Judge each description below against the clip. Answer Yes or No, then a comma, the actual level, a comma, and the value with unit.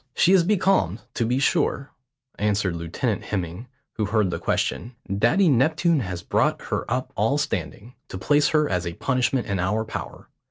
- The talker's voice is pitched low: Yes, low, 115 Hz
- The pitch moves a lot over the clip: Yes, wide, 7.4 semitones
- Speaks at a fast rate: No, average, 170 wpm